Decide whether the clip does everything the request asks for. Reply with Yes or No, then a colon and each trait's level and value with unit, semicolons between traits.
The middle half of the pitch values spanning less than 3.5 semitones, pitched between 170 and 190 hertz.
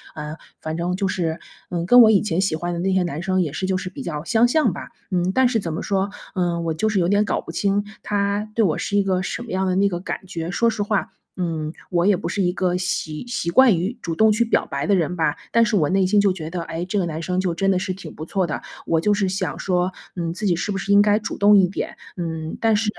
Yes: average, 3.0 semitones; medium, 185 Hz